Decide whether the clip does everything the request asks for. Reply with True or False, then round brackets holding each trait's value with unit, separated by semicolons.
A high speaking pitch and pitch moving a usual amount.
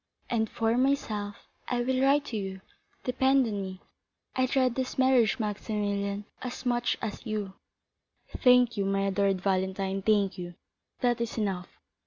True (215 Hz; 4.1 semitones)